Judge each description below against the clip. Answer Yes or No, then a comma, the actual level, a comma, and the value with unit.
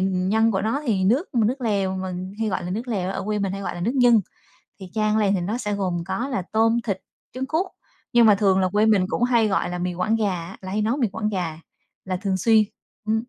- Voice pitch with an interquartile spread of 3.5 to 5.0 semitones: No, average, 3.1 semitones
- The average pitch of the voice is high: Yes, high, 210 Hz